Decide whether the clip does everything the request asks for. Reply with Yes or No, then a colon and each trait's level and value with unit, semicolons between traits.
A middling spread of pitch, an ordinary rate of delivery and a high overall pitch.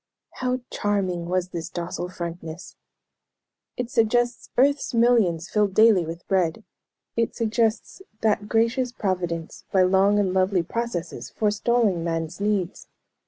No: average, 4.6 semitones; slow, 120 wpm; high, 195 Hz